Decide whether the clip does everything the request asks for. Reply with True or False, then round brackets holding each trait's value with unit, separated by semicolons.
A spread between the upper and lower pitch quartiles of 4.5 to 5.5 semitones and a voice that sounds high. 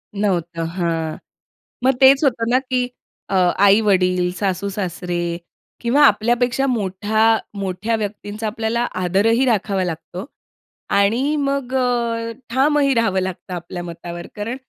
True (4.8 semitones; 210 Hz)